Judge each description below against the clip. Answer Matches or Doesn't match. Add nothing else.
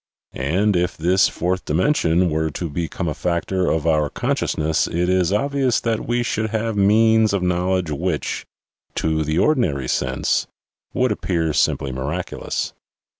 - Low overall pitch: Matches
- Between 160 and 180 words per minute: Doesn't match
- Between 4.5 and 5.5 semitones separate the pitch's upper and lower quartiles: Matches